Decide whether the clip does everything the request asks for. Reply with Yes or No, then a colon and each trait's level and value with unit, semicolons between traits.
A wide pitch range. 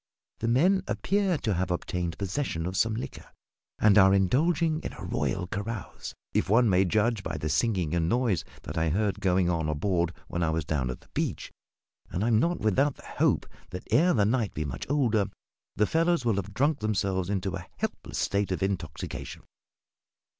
No: average, 5.0 semitones